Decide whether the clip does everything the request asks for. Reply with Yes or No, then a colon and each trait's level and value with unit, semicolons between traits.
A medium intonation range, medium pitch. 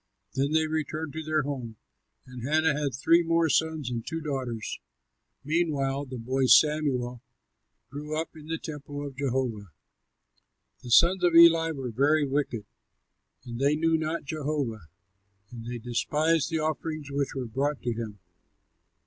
Yes: average, 3.7 semitones; medium, 145 Hz